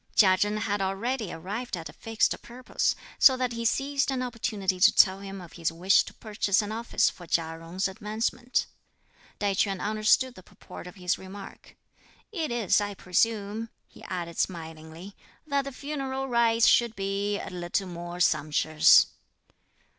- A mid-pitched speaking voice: No, high, 205 Hz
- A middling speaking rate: Yes, average, 160 wpm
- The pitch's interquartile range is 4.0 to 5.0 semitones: Yes, average, 4.4 semitones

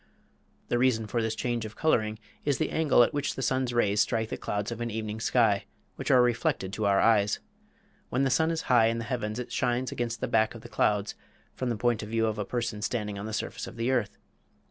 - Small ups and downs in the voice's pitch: Yes, narrow, 2.3 semitones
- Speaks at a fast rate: Yes, fast, 240 wpm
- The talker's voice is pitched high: No, low, 115 Hz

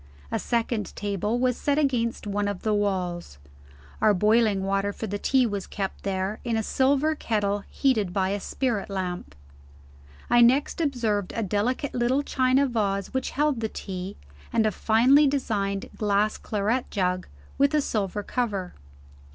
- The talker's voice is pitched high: Yes, high, 215 Hz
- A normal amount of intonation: Yes, average, 4.1 semitones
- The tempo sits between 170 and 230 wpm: No, average, 160 wpm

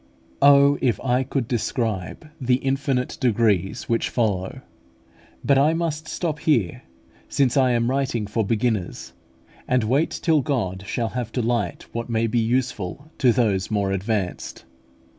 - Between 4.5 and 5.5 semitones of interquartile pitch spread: No, average, 3.9 semitones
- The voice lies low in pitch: Yes, low, 120 Hz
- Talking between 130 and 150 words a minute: Yes, average, 145 wpm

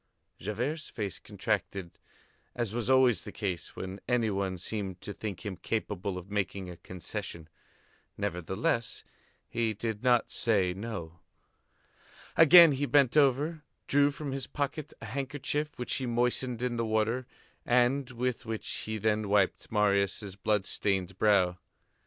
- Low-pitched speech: Yes, low, 110 Hz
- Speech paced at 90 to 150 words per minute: Yes, average, 140 wpm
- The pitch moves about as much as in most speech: Yes, average, 4.4 semitones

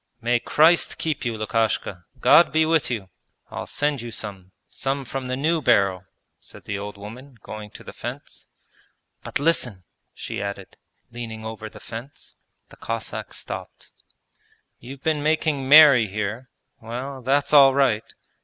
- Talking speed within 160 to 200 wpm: No, average, 150 wpm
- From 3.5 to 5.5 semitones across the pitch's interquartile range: Yes, average, 4.7 semitones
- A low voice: Yes, low, 120 Hz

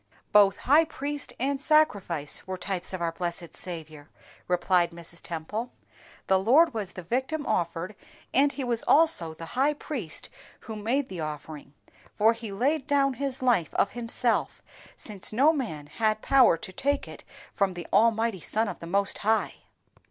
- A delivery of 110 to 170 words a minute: Yes, average, 165 wpm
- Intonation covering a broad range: Yes, wide, 7.4 semitones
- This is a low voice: No, high, 215 Hz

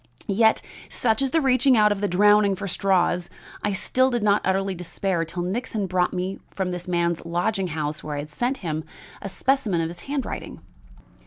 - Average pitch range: Yes, average, 4.0 semitones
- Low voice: No, high, 195 Hz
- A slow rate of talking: No, average, 185 wpm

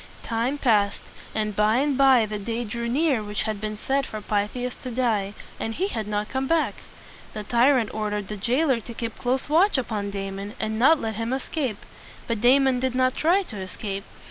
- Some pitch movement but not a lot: Yes, average, 3.8 semitones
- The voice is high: Yes, high, 230 Hz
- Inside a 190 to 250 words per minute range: Yes, average, 195 wpm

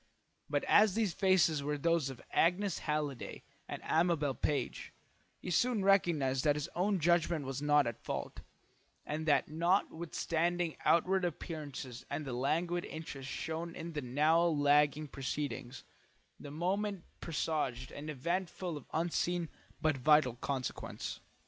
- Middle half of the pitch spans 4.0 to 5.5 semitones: No, average, 3.2 semitones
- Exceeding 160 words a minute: No, slow, 135 wpm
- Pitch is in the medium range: Yes, medium, 155 Hz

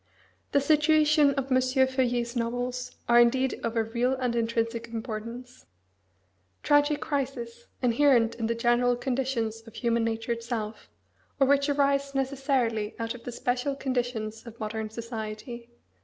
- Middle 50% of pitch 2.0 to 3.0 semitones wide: Yes, narrow, 2.6 semitones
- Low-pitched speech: No, high, 245 Hz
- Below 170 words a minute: Yes, average, 140 wpm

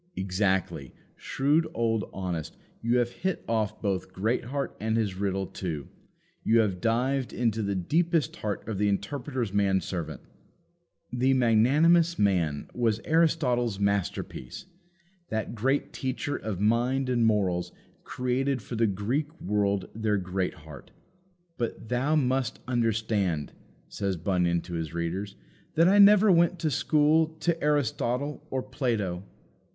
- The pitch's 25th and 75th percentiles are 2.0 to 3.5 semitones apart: No, wide, 5.6 semitones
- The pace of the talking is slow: Yes, slow, 130 wpm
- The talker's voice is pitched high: No, low, 115 Hz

